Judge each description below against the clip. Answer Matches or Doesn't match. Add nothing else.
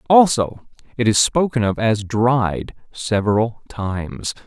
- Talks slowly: Matches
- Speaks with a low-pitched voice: Matches